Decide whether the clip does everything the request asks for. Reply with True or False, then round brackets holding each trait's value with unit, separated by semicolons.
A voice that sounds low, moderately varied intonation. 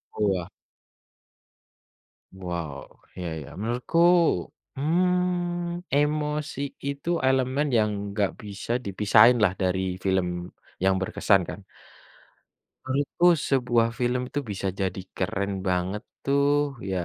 False (115 Hz; 7.1 semitones)